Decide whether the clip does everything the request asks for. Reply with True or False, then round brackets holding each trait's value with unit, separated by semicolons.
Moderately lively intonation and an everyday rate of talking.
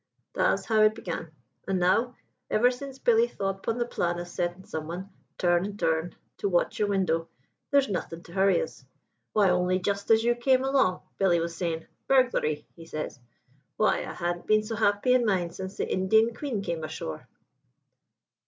True (4.6 semitones; 180 wpm)